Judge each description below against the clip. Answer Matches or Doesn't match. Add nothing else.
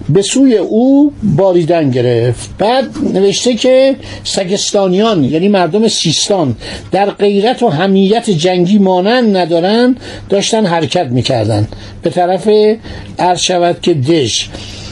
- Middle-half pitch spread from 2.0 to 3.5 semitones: Doesn't match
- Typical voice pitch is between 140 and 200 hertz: Matches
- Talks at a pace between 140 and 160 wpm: Doesn't match